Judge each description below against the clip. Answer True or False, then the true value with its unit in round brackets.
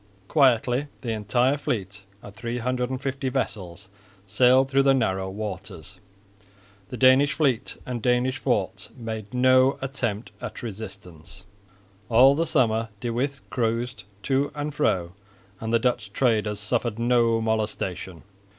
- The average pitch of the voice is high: False (120 Hz)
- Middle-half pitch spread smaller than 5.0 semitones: True (3.8 semitones)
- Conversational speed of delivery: False (125 wpm)